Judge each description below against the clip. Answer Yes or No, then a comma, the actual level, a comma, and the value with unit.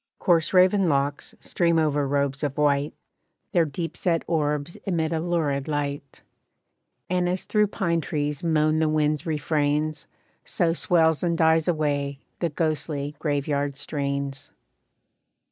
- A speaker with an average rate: No, slow, 130 wpm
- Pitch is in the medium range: Yes, medium, 155 Hz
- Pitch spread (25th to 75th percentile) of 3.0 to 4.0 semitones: No, narrow, 2.6 semitones